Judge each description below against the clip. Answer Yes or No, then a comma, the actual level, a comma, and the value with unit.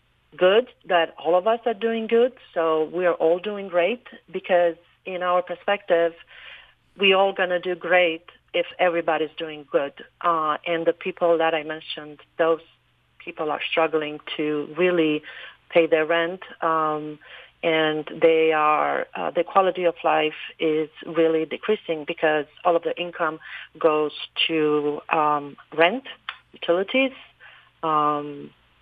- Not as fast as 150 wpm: Yes, average, 140 wpm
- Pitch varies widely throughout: No, narrow, 2.6 semitones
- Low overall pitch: No, medium, 165 Hz